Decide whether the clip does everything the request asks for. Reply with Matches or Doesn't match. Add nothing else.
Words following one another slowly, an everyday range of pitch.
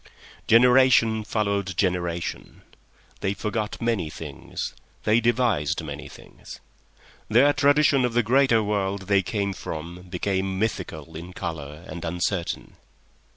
Matches